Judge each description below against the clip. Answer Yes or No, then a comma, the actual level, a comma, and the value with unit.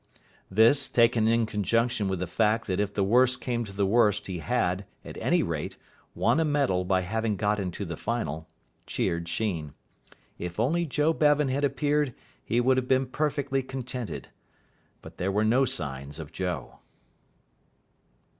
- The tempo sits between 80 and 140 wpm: No, average, 165 wpm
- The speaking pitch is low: Yes, low, 110 Hz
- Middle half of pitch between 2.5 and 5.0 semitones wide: No, wide, 5.5 semitones